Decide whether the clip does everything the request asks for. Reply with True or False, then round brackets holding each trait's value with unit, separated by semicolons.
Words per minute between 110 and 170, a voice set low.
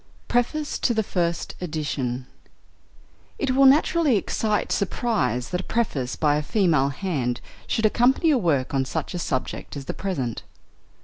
False (150 wpm; 180 Hz)